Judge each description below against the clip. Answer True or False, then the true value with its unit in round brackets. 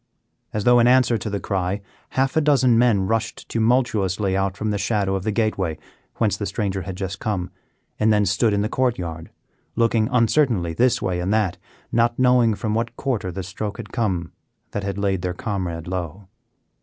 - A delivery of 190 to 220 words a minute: True (195 wpm)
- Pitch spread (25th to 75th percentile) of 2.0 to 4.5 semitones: True (3.6 semitones)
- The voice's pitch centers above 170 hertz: False (105 Hz)